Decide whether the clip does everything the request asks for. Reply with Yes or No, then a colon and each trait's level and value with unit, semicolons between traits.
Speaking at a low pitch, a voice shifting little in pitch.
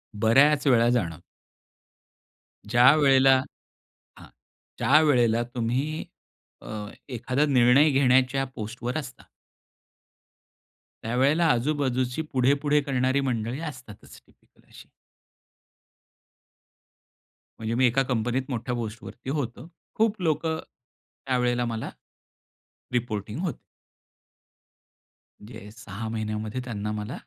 No: low, 125 Hz; average, 3.2 semitones